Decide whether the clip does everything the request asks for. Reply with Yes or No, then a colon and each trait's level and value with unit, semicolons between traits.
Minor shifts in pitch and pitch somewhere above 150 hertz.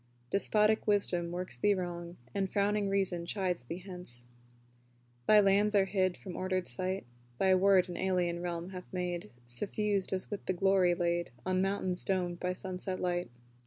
Yes: narrow, 1.9 semitones; medium, 185 Hz